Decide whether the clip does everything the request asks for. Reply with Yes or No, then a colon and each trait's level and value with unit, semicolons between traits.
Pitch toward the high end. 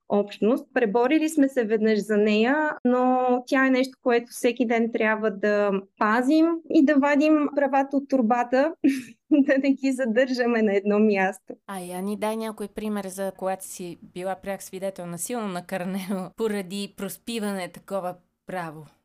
Yes: high, 220 Hz